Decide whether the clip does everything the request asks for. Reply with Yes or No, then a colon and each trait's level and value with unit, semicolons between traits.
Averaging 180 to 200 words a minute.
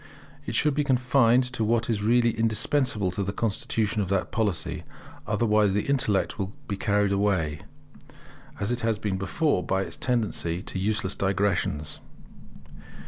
No: average, 150 wpm